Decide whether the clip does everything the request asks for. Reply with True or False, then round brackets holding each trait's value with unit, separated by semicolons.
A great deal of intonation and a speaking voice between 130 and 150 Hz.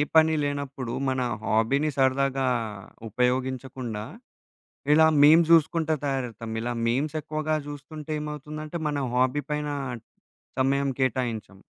False (2.9 semitones; 140 Hz)